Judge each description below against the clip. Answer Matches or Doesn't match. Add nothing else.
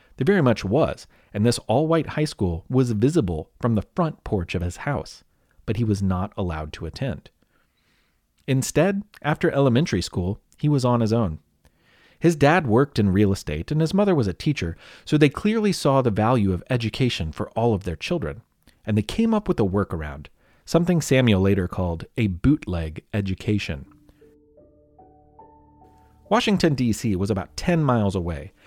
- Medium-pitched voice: Doesn't match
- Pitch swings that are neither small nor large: Doesn't match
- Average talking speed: Matches